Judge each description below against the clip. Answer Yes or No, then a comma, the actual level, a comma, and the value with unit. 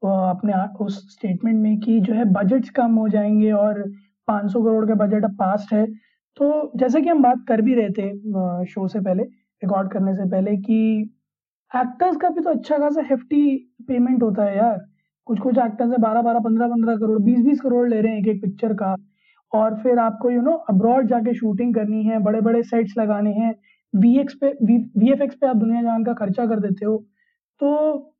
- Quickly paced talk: No, average, 165 wpm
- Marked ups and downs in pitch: No, average, 2.9 semitones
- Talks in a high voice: Yes, high, 225 Hz